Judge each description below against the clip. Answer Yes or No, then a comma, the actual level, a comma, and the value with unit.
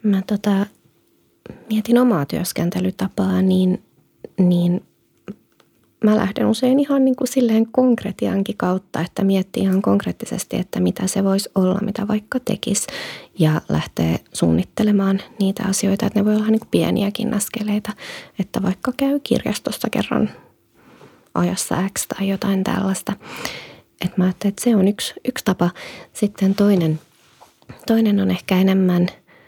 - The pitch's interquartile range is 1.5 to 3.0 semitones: Yes, average, 2.7 semitones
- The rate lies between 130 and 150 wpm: Yes, average, 135 wpm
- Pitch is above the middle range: Yes, high, 200 Hz